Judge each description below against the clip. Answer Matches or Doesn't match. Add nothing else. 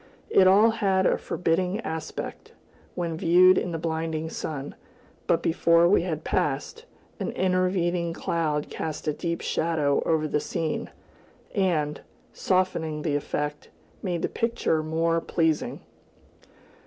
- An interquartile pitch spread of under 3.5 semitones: Matches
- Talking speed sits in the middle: Doesn't match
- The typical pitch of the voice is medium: Matches